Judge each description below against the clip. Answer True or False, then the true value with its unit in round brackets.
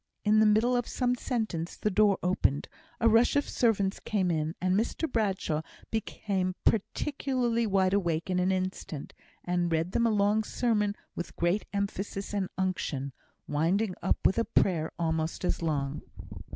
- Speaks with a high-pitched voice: True (195 Hz)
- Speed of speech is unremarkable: True (160 wpm)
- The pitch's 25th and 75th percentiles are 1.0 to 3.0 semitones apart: False (4.1 semitones)